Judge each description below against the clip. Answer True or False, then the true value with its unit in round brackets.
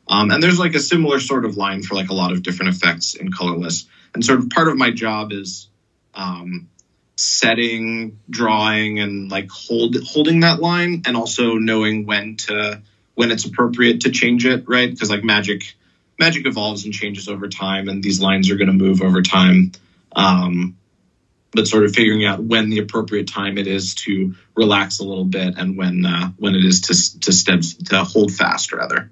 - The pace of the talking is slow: False (195 wpm)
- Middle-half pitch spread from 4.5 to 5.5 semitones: False (3.4 semitones)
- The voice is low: True (105 Hz)